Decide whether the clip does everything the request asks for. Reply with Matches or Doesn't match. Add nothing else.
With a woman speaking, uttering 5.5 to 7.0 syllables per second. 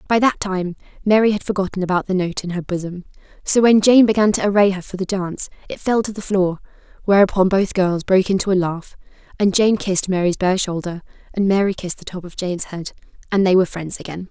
Matches